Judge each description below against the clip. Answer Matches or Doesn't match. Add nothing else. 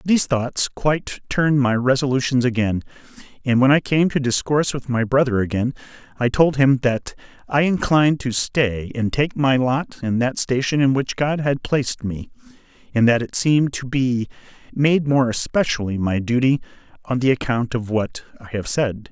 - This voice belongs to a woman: Doesn't match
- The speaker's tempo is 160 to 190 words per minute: Matches